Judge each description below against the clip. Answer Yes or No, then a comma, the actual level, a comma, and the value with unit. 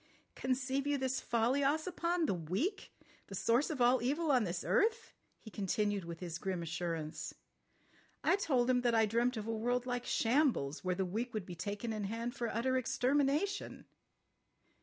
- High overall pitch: Yes, high, 240 Hz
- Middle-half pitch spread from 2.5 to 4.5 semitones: No, average, 5.2 semitones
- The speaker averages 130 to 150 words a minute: No, average, 175 wpm